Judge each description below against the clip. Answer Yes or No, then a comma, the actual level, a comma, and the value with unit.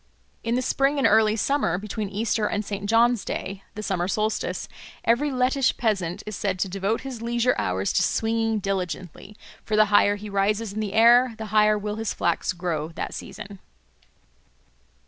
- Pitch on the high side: Yes, high, 215 Hz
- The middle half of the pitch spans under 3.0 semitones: Yes, narrow, 2.5 semitones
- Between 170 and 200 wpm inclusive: Yes, average, 175 wpm